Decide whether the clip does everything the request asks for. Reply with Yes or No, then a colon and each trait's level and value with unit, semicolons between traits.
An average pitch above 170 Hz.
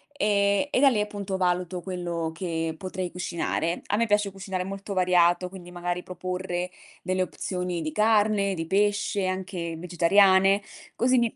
Yes: medium, 185 Hz